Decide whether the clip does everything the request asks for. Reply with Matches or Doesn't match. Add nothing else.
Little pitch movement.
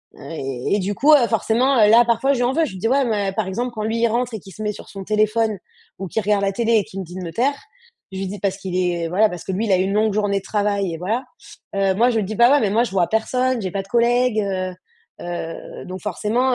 Doesn't match